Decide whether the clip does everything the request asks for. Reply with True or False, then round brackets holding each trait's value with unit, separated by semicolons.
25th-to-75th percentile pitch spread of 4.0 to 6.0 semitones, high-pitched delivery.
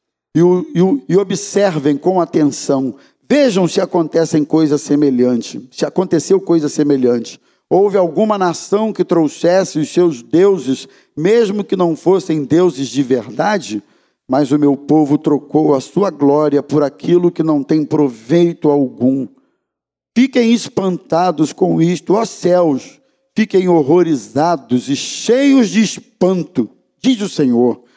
False (4.8 semitones; 165 Hz)